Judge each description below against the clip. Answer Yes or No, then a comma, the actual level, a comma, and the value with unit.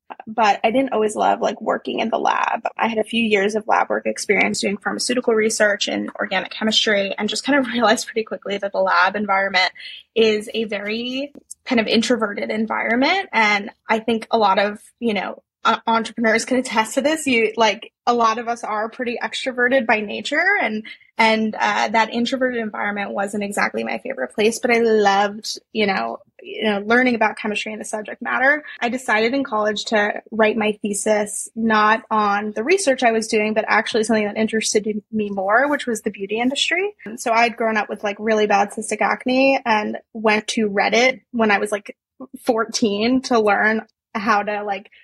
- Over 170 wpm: Yes, average, 190 wpm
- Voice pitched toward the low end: No, high, 220 Hz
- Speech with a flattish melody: Yes, narrow, 2.2 semitones